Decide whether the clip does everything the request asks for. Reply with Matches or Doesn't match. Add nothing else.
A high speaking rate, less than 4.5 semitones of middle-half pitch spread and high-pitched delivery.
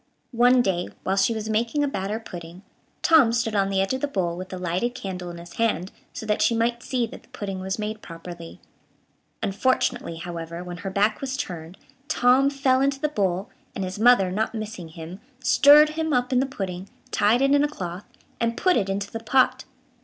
Doesn't match